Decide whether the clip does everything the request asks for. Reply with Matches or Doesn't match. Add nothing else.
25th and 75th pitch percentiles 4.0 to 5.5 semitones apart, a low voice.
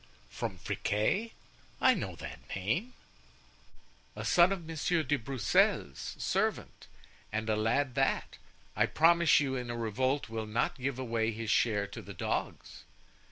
Matches